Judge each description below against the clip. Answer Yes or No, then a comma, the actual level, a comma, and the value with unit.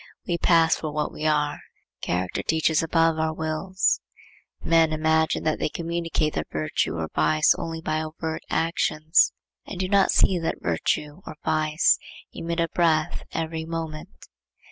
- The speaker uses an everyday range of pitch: No, narrow, 1.2 semitones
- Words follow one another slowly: No, average, 150 wpm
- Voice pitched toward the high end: No, medium, 160 Hz